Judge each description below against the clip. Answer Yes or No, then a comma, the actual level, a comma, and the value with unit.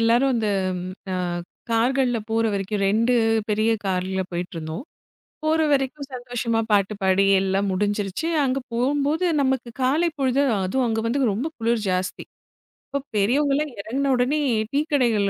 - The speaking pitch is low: No, high, 235 Hz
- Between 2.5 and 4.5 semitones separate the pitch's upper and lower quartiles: No, average, 5.1 semitones